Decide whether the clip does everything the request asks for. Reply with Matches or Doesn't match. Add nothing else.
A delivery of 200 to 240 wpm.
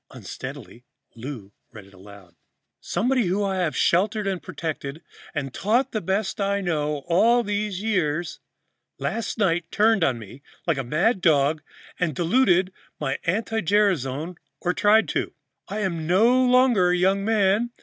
Doesn't match